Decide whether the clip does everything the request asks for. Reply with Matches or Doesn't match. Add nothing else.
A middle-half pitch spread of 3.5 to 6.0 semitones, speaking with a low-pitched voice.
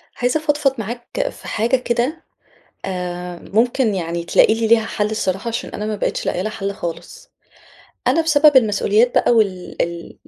Doesn't match